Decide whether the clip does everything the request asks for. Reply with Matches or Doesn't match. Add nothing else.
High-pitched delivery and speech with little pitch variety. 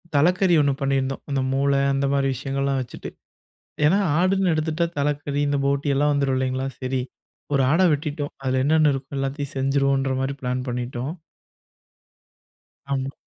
Doesn't match